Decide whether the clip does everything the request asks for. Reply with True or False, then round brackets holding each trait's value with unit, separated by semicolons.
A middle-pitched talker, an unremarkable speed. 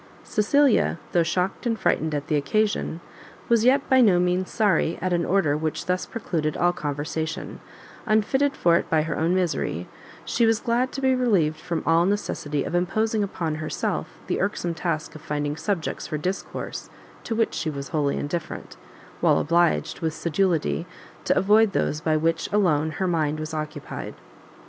True (170 Hz; 170 wpm)